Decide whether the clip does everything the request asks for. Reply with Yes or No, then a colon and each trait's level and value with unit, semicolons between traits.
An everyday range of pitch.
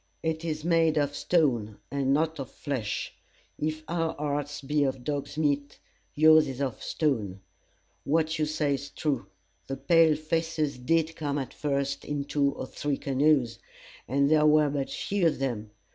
No: narrow, 2.2 semitones